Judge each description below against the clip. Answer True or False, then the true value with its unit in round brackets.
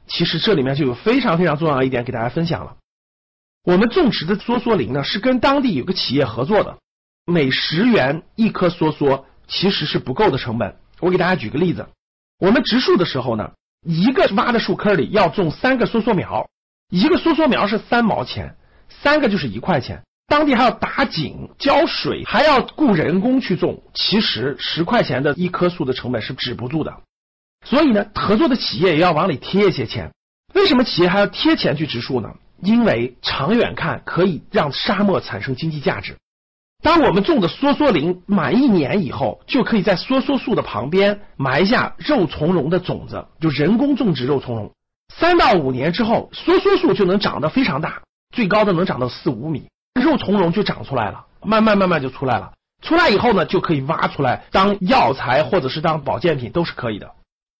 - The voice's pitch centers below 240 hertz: True (185 Hz)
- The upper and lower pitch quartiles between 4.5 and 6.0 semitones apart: False (7.3 semitones)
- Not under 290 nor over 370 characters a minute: True (295 characters per minute)